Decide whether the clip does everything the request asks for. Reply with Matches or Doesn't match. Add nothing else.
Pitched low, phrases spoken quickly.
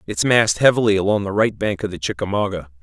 Matches